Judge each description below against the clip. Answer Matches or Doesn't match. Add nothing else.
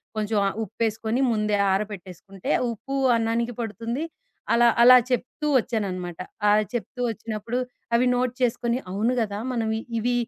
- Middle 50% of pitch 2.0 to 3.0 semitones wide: Matches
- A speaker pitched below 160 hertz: Doesn't match